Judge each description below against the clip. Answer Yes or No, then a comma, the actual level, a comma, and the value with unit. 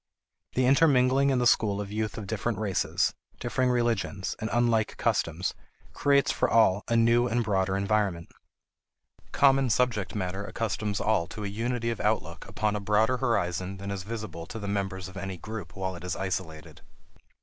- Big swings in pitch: No, average, 3.6 semitones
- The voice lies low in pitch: Yes, low, 105 Hz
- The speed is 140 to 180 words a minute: Yes, average, 170 wpm